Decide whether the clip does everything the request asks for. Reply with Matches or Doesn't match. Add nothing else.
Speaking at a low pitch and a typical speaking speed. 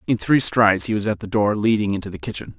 Doesn't match